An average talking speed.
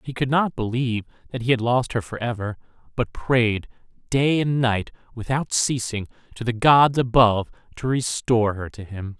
Yes: average, 175 wpm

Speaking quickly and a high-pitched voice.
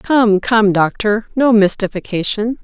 No: slow, 115 wpm; high, 215 Hz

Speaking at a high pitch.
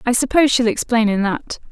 Yes: high, 235 Hz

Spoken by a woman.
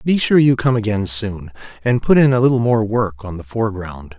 No: male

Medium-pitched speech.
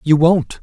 Yes: medium, 155 Hz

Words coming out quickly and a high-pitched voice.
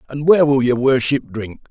No: fast, 210 wpm; low, 130 Hz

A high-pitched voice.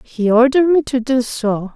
Yes: very high, 250 Hz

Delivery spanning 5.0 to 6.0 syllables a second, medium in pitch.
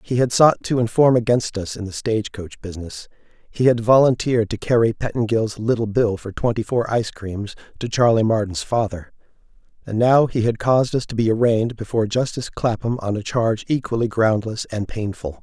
No: 5.6 syllables/s; low, 110 Hz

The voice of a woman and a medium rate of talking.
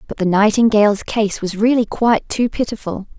Yes: female; average, 170 wpm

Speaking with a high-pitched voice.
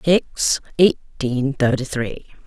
No: medium, 140 Hz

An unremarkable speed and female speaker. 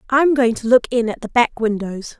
No: fast, 245 wpm; female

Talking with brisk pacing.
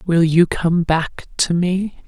No: average, 175 wpm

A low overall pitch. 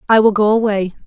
No: high, 210 Hz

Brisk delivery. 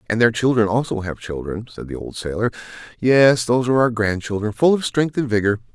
Yes: fast, 220 wpm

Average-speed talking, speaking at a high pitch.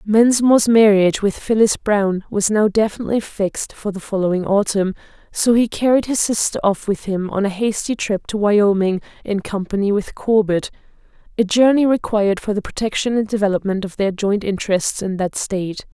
Yes: average, 170 wpm; high, 205 Hz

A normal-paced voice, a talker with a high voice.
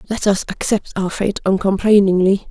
Yes: average, 145 wpm; high, 195 Hz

